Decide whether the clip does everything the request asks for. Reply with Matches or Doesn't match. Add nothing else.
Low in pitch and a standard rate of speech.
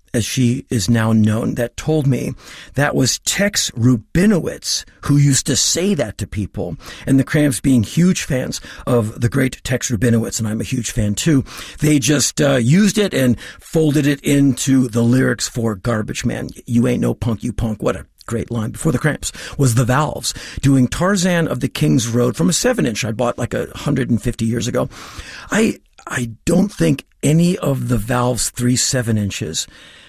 Matches